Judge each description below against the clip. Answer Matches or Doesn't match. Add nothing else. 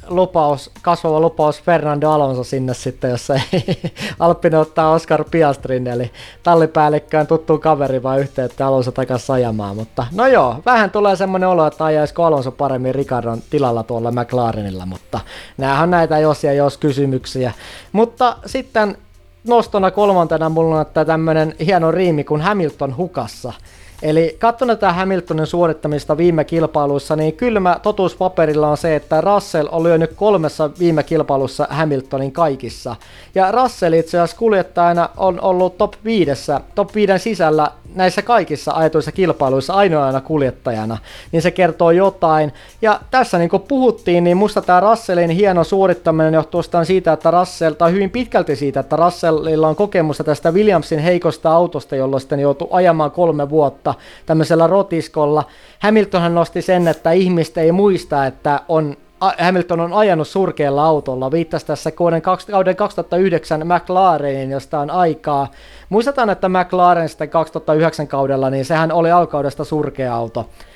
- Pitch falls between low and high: Matches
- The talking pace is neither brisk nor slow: Matches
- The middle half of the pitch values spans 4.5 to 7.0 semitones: Doesn't match